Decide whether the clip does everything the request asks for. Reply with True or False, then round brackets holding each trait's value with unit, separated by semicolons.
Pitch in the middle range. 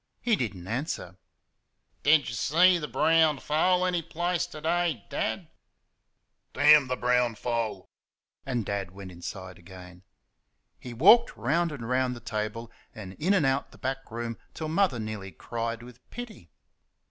False (125 Hz)